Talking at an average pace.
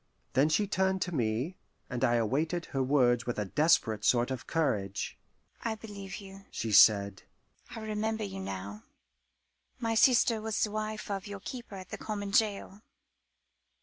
Yes: average, 160 wpm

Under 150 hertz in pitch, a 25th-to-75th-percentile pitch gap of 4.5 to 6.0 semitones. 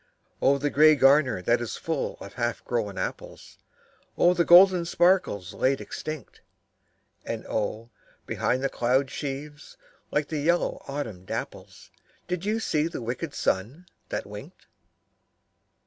Yes: medium, 140 Hz; wide, 5.5 semitones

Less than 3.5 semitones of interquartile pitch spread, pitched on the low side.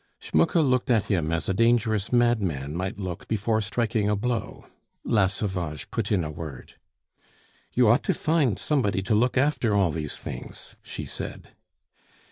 No: average, 4.7 semitones; low, 105 Hz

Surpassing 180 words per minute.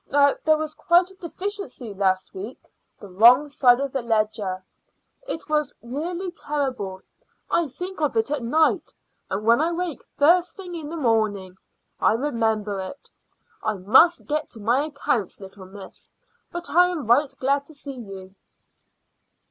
No: average, 160 wpm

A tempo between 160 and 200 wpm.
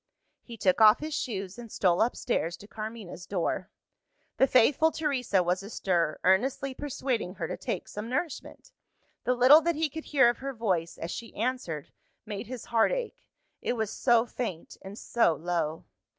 Yes: average, 170 wpm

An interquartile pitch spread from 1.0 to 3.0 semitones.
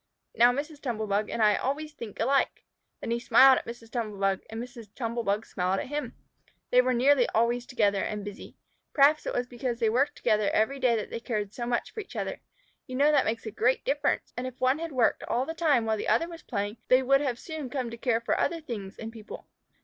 No: average, 3.7 semitones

